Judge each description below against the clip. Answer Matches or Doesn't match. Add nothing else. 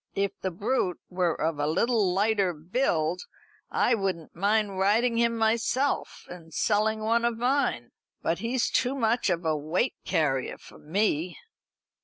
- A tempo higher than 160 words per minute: Doesn't match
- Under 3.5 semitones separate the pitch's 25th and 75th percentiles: Doesn't match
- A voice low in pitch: Doesn't match